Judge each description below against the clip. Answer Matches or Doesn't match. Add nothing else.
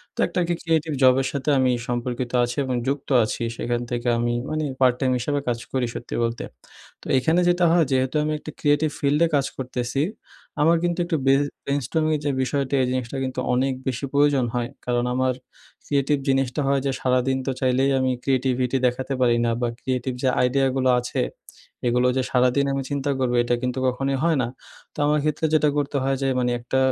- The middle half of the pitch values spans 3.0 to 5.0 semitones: Doesn't match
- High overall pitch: Doesn't match